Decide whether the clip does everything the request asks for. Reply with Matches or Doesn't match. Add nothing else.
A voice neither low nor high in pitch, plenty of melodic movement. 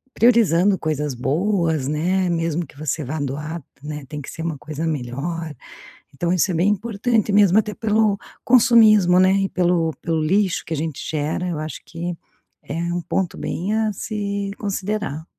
Doesn't match